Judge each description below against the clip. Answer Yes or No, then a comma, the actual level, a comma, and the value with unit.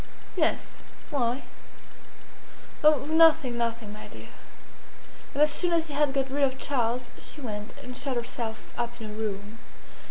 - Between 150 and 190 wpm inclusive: Yes, average, 155 wpm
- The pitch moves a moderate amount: Yes, average, 4.1 semitones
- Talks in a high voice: Yes, very high, 250 Hz